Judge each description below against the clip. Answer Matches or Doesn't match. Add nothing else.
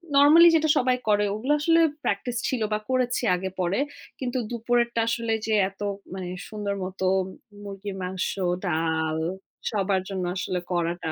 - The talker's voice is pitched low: Doesn't match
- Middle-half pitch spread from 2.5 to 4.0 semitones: Doesn't match